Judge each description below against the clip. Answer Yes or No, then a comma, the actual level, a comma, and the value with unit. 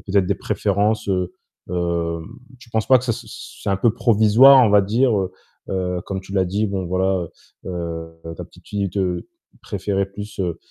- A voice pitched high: No, very low, 95 Hz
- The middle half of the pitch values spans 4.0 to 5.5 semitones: No, average, 2.9 semitones